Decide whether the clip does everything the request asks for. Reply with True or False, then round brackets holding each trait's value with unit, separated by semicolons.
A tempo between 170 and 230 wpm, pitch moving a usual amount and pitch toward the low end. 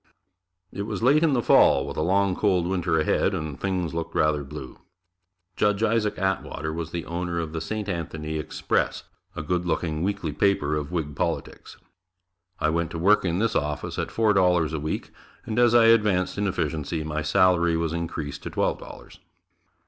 True (185 wpm; 4.1 semitones; 85 Hz)